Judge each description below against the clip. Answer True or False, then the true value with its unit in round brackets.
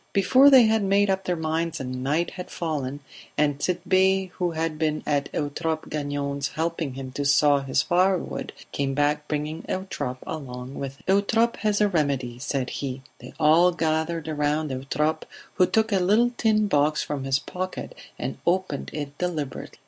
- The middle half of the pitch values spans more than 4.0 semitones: True (4.6 semitones)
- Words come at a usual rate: True (165 wpm)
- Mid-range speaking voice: True (155 Hz)